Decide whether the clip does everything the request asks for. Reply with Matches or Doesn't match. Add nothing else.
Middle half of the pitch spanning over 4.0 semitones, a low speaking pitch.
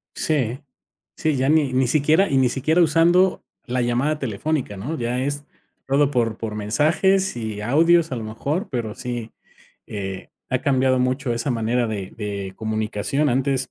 Matches